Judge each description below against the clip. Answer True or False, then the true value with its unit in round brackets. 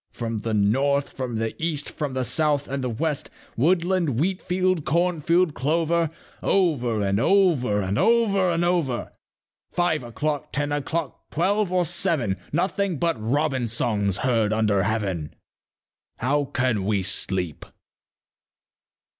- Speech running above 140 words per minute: False (135 wpm)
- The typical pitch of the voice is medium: True (145 Hz)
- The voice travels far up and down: True (7.0 semitones)